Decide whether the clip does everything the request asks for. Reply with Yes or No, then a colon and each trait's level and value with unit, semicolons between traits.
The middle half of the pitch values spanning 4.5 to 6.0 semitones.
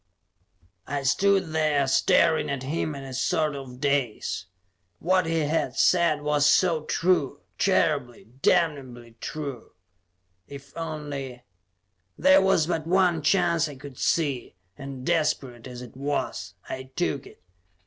No: average, 3.5 semitones